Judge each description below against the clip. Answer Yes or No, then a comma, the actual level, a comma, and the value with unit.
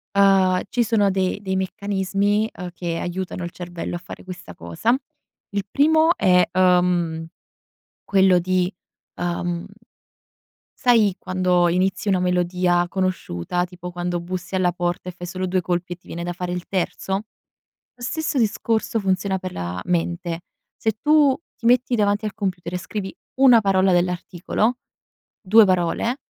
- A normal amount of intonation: No, narrow, 2.3 semitones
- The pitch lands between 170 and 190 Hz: Yes, medium, 185 Hz